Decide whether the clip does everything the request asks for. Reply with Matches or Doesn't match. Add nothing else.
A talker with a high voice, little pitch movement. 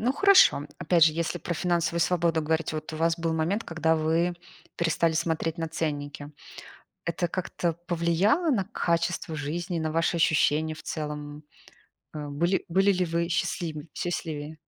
Doesn't match